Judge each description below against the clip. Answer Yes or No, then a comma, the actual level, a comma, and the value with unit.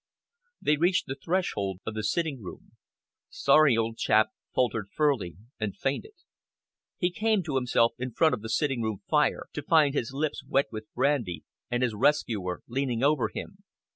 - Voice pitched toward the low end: Yes, low, 130 Hz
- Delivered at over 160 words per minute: Yes, average, 170 wpm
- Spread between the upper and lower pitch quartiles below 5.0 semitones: No, wide, 5.4 semitones